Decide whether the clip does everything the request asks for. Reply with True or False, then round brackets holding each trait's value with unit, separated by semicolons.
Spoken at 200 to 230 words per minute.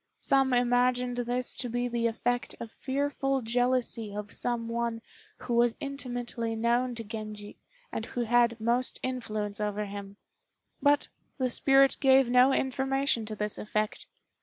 False (145 wpm)